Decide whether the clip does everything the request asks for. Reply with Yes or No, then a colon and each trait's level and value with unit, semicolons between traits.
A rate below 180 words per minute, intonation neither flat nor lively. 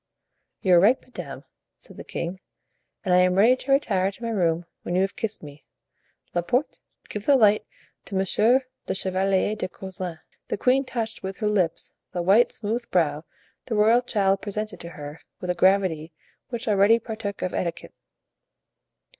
Yes: average, 170 wpm; average, 3.7 semitones